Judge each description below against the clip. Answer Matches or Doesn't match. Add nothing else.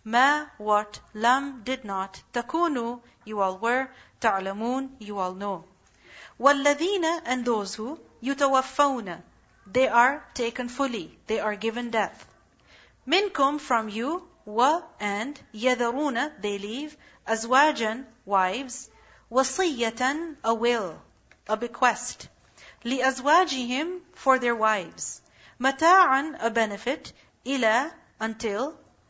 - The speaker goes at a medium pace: Doesn't match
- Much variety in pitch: Doesn't match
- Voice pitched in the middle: Doesn't match